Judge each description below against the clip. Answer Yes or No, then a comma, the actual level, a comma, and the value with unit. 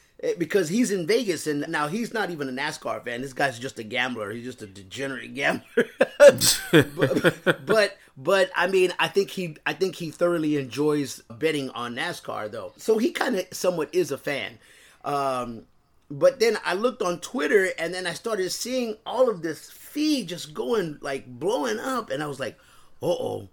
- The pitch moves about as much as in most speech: No, wide, 6.9 semitones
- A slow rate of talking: No, average, 185 wpm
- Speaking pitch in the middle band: Yes, medium, 170 Hz